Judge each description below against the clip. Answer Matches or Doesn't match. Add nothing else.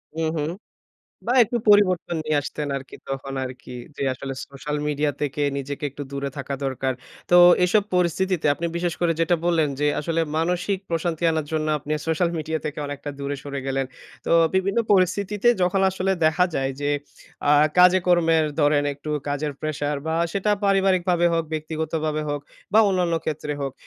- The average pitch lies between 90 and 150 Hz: Doesn't match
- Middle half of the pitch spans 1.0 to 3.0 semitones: Doesn't match